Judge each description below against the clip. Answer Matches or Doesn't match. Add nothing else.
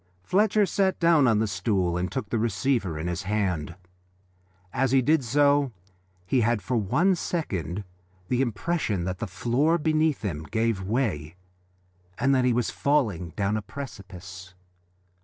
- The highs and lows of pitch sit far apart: Matches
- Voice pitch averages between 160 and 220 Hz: Doesn't match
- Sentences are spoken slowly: Doesn't match